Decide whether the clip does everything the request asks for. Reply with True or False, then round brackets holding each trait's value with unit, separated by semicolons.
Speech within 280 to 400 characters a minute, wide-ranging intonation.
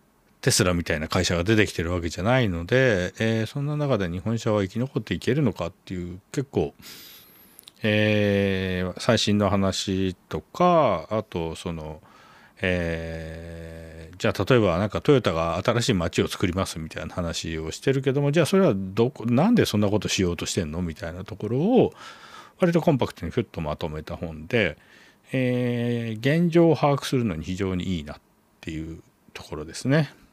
True (340 characters per minute; 6.2 semitones)